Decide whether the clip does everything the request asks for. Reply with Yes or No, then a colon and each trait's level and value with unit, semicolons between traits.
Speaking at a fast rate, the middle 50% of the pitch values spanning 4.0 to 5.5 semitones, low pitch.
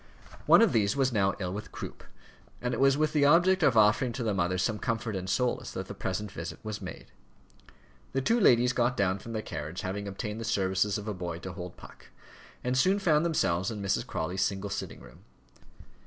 Yes: fast, 215 wpm; average, 5.1 semitones; low, 105 Hz